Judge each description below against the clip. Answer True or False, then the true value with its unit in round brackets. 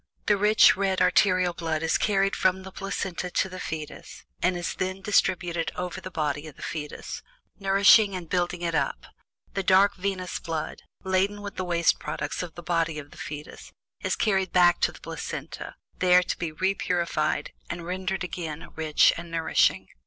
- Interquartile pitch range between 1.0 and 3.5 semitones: True (2.4 semitones)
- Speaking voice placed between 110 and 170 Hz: False (180 Hz)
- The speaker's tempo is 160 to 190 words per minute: True (175 wpm)